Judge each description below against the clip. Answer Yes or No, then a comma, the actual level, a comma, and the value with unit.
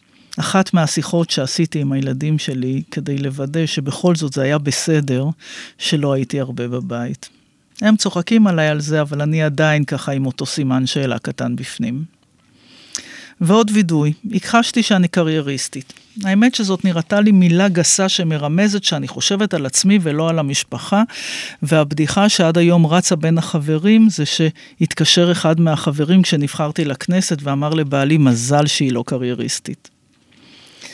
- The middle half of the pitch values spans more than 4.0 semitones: Yes, average, 4.4 semitones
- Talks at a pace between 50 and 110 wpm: No, average, 135 wpm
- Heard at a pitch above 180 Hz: No, medium, 155 Hz